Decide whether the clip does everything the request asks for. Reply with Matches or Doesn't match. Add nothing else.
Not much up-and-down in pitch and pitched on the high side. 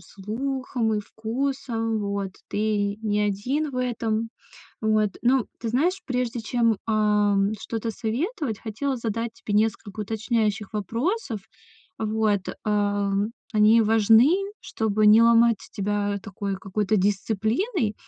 Matches